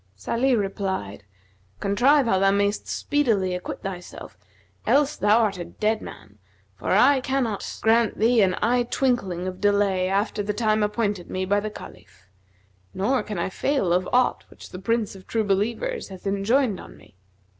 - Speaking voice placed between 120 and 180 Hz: No, high, 205 Hz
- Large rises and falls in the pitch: No, average, 3.8 semitones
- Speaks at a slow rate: No, average, 165 wpm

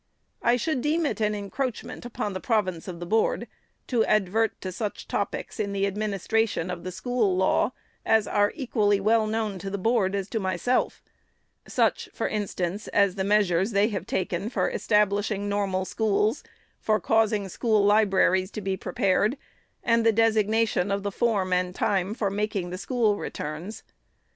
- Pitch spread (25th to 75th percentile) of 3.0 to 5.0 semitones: No, narrow, 2.6 semitones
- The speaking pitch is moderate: No, high, 205 Hz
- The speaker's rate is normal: Yes, average, 175 wpm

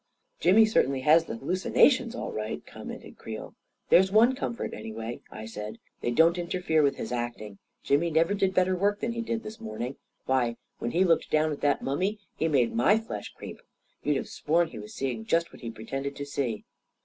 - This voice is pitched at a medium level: Yes, medium, 155 Hz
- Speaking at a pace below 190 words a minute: No, fast, 205 wpm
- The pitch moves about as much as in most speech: No, wide, 7.8 semitones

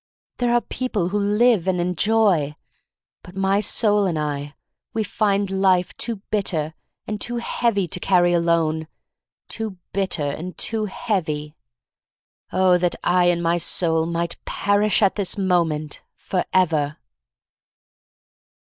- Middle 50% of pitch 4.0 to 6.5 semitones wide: No, average, 3.5 semitones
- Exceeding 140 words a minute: No, slow, 135 wpm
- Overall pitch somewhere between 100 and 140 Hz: No, medium, 185 Hz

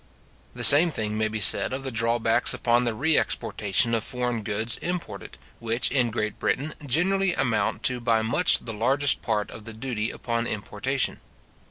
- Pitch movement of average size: Yes, average, 3.3 semitones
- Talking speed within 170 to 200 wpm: Yes, average, 175 wpm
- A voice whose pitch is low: Yes, low, 120 Hz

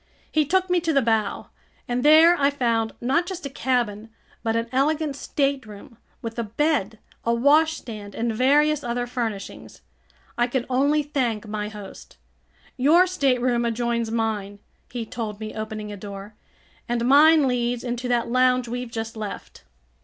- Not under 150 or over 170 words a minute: Yes, average, 155 wpm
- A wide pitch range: No, average, 4.0 semitones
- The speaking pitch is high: Yes, high, 245 Hz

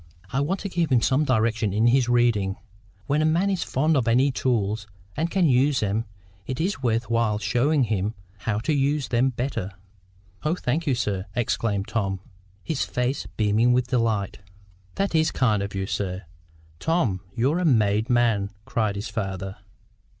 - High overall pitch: No, low, 120 Hz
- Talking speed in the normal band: Yes, average, 170 wpm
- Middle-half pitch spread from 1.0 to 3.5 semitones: No, average, 5.0 semitones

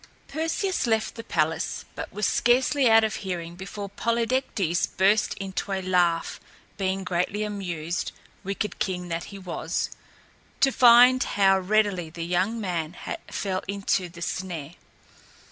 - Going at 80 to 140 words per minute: Yes, slow, 135 wpm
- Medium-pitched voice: No, high, 195 Hz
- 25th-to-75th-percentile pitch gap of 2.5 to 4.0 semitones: Yes, average, 3.7 semitones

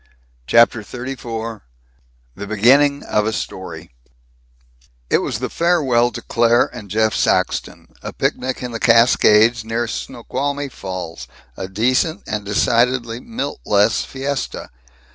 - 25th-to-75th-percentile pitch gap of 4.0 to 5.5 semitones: No, average, 3.3 semitones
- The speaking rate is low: Yes, slow, 125 wpm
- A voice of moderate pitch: No, low, 115 Hz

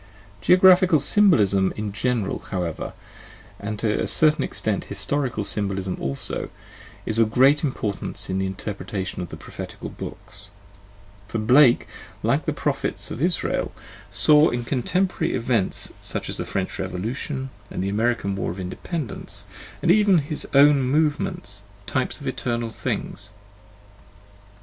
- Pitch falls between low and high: No, low, 120 Hz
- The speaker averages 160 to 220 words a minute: No, average, 140 wpm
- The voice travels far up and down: Yes, wide, 6.8 semitones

